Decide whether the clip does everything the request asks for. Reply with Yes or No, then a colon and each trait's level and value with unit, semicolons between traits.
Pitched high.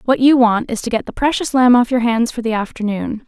Yes: high, 240 Hz